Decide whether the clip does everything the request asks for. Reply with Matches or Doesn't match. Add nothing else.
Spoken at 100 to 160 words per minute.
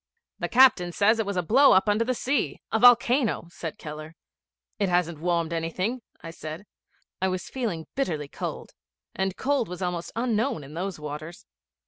Doesn't match